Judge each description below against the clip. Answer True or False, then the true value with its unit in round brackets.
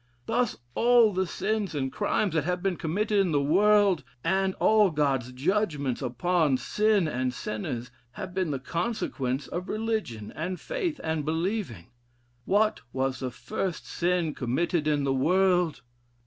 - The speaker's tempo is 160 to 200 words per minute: False (150 wpm)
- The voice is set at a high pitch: False (175 Hz)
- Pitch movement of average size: False (6.7 semitones)